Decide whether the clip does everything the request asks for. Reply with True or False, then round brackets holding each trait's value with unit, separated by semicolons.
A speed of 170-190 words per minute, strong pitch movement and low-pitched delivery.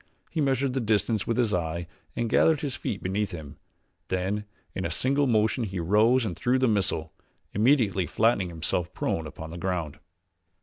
True (175 wpm; 5.7 semitones; 105 Hz)